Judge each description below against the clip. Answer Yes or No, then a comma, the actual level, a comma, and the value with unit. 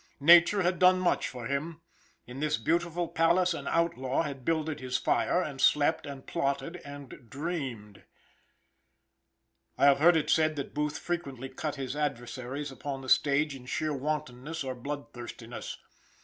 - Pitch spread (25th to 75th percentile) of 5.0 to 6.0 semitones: No, average, 3.7 semitones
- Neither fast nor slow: Yes, average, 150 wpm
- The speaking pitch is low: No, medium, 145 Hz